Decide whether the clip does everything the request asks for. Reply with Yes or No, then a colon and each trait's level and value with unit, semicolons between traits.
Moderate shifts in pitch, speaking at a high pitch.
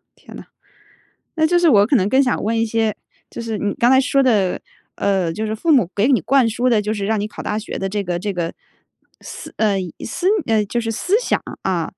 Yes: average, 3.7 semitones; high, 220 Hz